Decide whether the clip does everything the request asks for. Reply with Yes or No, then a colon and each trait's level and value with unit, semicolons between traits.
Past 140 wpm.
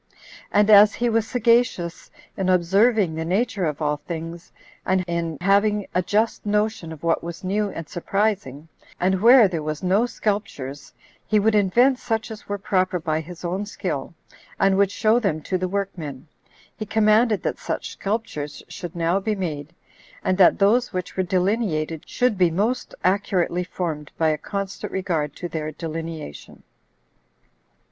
Yes: average, 160 wpm